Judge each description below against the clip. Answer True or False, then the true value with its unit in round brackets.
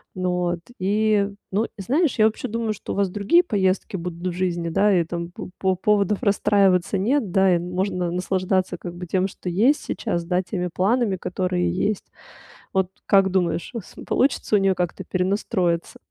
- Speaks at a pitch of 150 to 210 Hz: True (190 Hz)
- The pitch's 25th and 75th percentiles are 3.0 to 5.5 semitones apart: False (2.5 semitones)